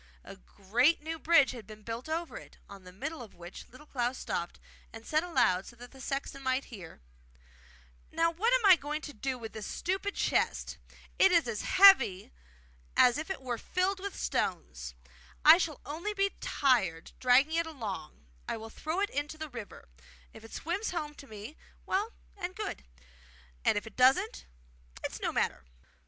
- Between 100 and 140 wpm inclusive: No, average, 180 wpm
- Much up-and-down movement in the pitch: Yes, wide, 7.0 semitones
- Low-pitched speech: No, very high, 275 Hz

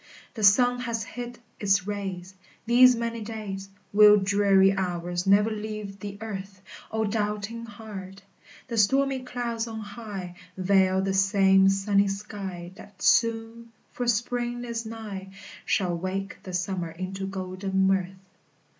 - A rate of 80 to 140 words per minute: Yes, slow, 135 wpm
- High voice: Yes, high, 200 Hz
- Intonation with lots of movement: No, average, 2.8 semitones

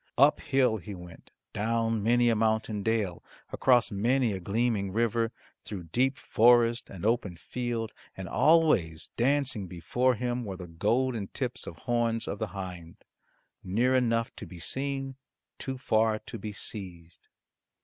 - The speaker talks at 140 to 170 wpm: Yes, average, 150 wpm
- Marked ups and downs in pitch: No, average, 3.9 semitones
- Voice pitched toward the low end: Yes, low, 115 Hz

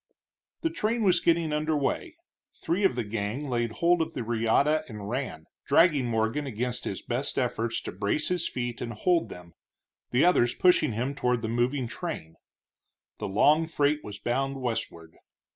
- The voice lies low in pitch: Yes, low, 125 Hz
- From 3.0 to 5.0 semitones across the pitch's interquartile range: No, wide, 5.5 semitones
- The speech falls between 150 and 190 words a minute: Yes, average, 170 wpm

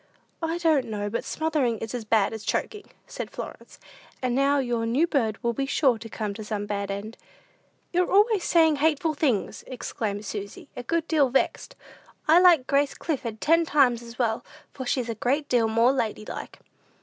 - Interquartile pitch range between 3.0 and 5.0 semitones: No, wide, 5.6 semitones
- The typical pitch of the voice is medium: No, very high, 250 Hz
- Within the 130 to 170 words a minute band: No, average, 185 wpm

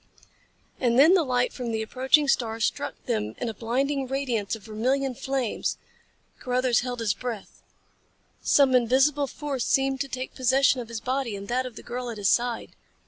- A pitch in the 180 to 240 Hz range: No, very high, 250 Hz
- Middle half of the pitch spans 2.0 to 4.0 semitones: Yes, average, 2.8 semitones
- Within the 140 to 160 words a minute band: No, average, 180 wpm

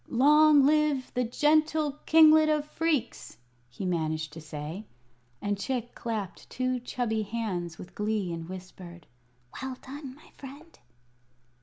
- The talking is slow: Yes, slow, 130 wpm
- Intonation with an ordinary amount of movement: No, wide, 8.1 semitones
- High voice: Yes, high, 245 Hz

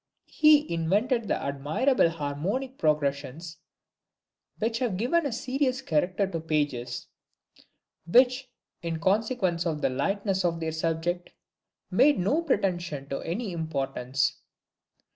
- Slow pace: Yes, slow, 115 wpm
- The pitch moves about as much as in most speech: No, wide, 7.6 semitones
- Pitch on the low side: No, medium, 175 Hz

